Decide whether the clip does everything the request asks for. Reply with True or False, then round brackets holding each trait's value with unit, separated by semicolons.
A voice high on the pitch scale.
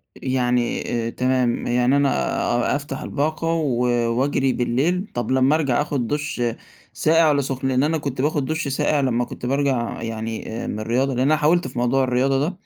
False (135 Hz)